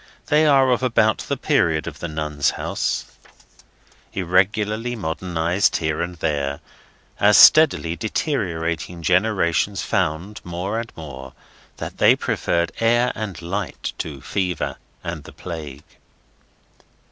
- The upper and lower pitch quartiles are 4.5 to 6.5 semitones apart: Yes, average, 5.1 semitones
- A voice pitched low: Yes, very low, 90 Hz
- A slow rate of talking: Yes, slow, 120 wpm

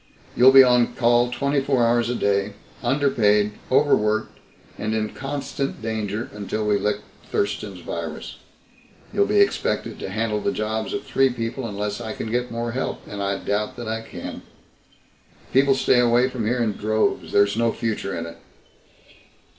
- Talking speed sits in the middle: Yes, average, 165 wpm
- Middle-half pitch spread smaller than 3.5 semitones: Yes, average, 2.9 semitones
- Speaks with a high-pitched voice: No, low, 115 Hz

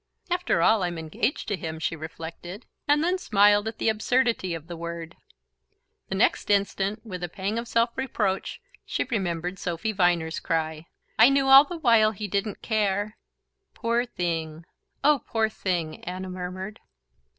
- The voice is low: No, high, 200 Hz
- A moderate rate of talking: Yes, average, 160 wpm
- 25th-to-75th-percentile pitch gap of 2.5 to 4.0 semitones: No, average, 4.8 semitones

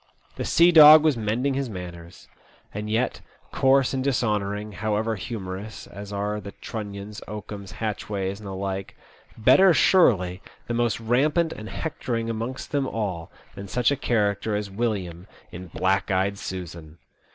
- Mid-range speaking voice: No, low, 105 Hz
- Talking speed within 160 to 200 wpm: No, average, 150 wpm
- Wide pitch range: No, average, 3.7 semitones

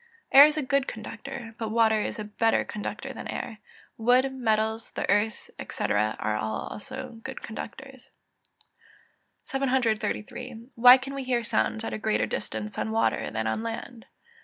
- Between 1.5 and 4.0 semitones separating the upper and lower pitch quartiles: Yes, average, 3.2 semitones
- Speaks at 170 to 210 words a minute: No, average, 160 wpm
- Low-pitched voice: No, high, 225 Hz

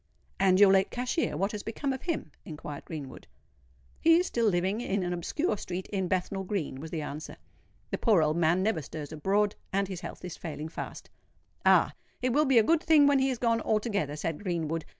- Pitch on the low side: No, high, 190 Hz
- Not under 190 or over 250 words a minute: Yes, fast, 205 wpm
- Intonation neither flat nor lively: No, wide, 6.0 semitones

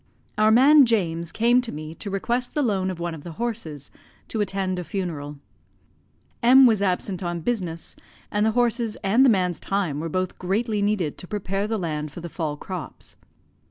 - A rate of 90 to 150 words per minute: No, average, 190 wpm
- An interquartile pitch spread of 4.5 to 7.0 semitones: Yes, average, 4.8 semitones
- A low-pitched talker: No, high, 195 Hz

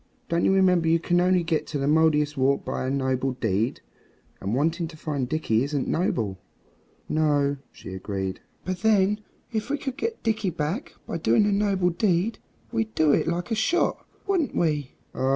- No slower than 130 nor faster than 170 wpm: No, average, 180 wpm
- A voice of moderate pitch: Yes, medium, 160 Hz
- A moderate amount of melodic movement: No, wide, 5.7 semitones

